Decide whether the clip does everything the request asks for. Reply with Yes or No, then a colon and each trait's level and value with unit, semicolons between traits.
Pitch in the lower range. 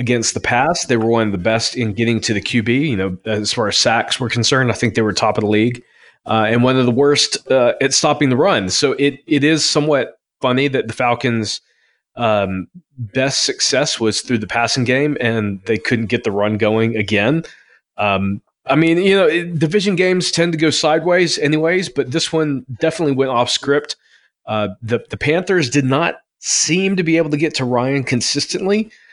Yes: low, 130 Hz